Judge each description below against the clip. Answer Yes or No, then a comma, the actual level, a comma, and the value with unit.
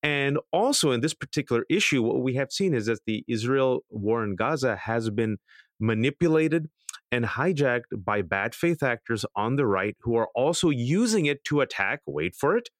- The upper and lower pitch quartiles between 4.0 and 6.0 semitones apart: Yes, wide, 5.4 semitones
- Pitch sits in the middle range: No, low, 130 Hz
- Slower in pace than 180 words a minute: No, average, 185 wpm